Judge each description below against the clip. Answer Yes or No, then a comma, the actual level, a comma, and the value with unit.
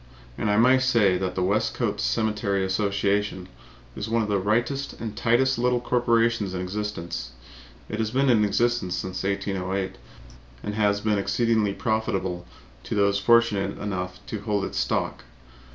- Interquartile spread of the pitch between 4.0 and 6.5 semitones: No, average, 3.2 semitones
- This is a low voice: Yes, low, 105 Hz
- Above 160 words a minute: No, average, 150 wpm